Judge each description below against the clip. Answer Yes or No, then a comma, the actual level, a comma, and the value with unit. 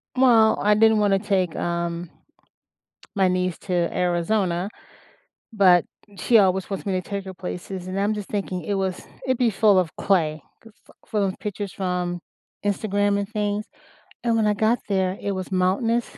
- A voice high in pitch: Yes, high, 195 Hz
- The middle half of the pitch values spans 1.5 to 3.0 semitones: Yes, narrow, 2.5 semitones